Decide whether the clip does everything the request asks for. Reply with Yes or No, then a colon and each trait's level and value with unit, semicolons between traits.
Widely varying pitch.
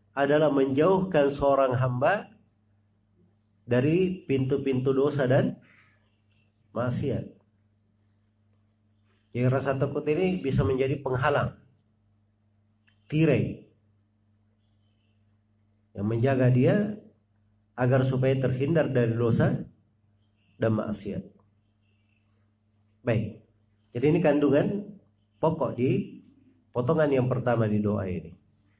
No: average, 4.5 semitones